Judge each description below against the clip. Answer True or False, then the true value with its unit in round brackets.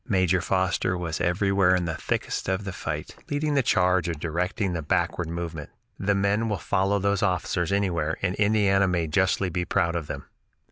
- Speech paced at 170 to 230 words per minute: True (185 wpm)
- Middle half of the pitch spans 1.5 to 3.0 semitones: True (2.5 semitones)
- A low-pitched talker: True (95 Hz)